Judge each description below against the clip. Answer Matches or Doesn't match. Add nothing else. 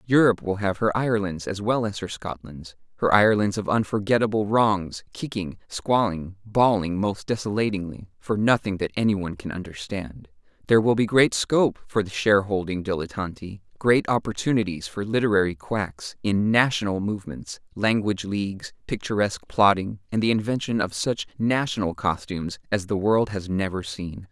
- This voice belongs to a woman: Doesn't match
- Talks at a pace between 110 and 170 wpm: Matches